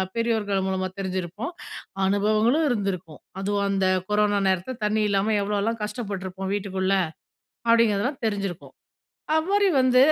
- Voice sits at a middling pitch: No, high, 205 Hz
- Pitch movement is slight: No, average, 3.0 semitones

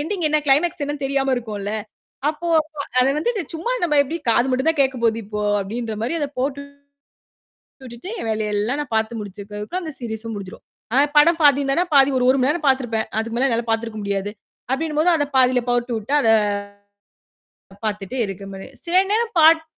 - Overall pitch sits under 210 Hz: No, very high, 255 Hz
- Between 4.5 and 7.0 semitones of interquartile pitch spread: Yes, average, 5.1 semitones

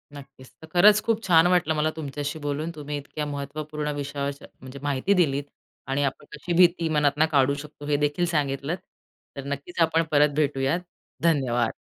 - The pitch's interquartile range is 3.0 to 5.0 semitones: No, narrow, 2.4 semitones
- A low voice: No, medium, 145 Hz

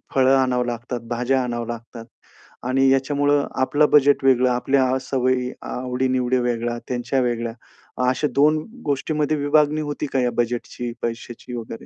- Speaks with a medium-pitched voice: No, low, 130 Hz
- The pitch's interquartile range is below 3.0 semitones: Yes, narrow, 2.4 semitones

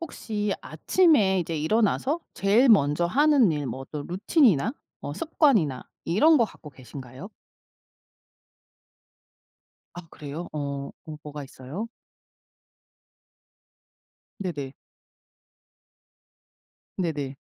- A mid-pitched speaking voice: Yes, medium, 175 Hz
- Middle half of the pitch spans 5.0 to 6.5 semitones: No, wide, 7.7 semitones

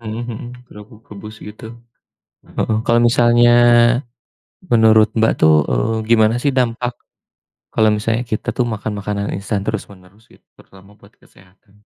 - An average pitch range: No, narrow, 2.2 semitones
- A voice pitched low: Yes, low, 110 Hz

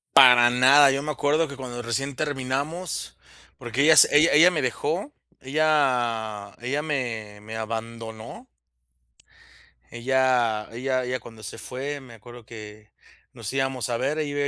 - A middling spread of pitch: Yes, average, 3.6 semitones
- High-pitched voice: No, low, 130 Hz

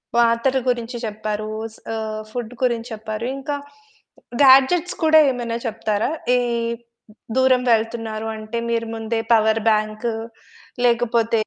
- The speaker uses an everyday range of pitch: No, narrow, 2.0 semitones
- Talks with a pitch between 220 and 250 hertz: Yes, high, 230 Hz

